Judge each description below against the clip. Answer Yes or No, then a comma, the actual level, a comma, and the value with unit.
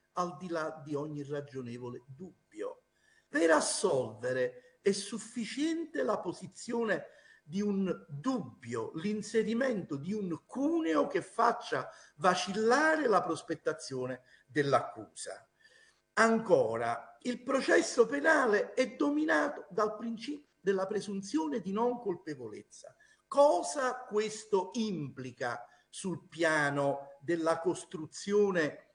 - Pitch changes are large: Yes, wide, 8.2 semitones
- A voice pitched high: Yes, high, 200 Hz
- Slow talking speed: Yes, slow, 95 wpm